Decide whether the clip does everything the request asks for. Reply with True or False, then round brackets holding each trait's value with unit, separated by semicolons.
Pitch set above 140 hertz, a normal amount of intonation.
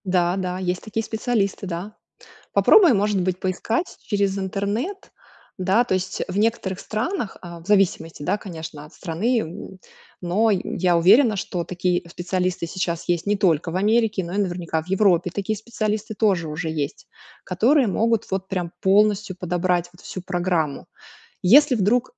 True (190 Hz; 3.2 semitones)